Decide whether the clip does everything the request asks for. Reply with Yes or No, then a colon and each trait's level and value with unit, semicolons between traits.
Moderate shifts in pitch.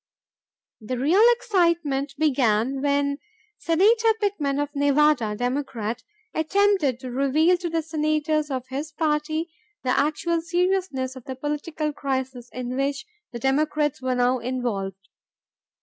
Yes: average, 3.6 semitones